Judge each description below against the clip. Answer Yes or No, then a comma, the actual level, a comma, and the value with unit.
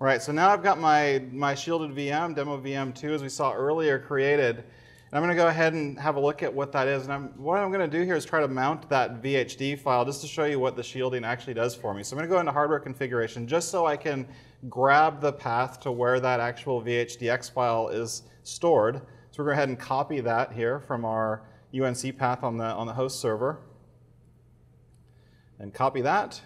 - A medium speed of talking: No, fast, 235 wpm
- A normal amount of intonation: Yes, average, 3.3 semitones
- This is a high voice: No, low, 135 Hz